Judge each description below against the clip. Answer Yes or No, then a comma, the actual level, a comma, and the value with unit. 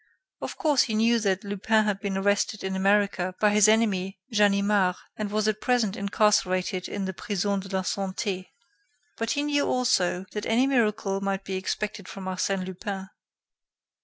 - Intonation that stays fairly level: Yes, narrow, 2.1 semitones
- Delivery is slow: No, average, 165 wpm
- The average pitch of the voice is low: No, high, 200 Hz